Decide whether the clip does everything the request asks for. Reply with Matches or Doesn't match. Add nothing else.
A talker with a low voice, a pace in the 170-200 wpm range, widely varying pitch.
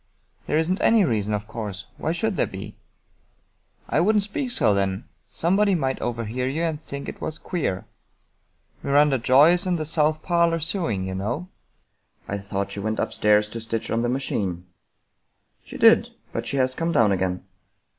Matches